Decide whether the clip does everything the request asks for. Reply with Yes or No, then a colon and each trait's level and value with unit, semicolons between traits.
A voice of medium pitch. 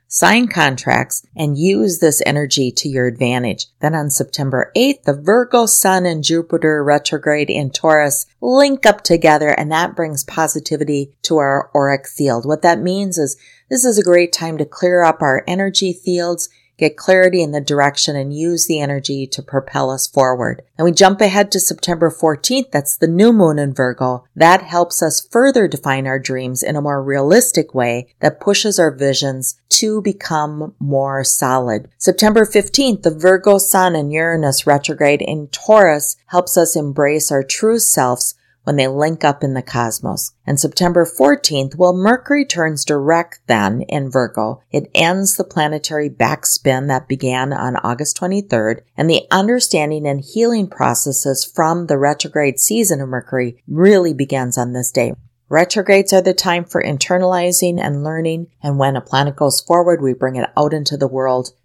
Yes: medium, 150 Hz